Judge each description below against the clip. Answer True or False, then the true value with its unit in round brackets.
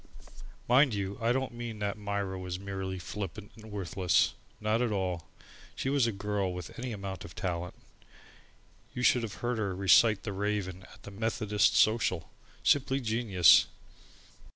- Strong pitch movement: False (3.2 semitones)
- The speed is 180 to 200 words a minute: False (155 wpm)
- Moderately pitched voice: False (105 Hz)